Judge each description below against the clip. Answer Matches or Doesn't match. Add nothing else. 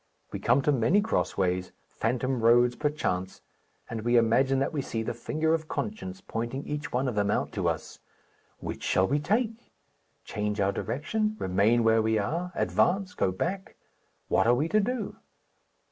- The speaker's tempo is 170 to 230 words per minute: Matches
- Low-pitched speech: Matches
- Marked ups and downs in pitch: Matches